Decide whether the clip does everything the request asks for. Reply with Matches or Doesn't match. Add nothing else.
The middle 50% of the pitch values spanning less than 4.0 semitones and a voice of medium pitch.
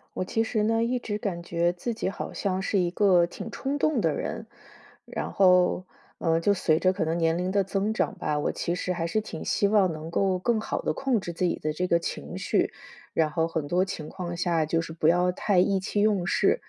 Matches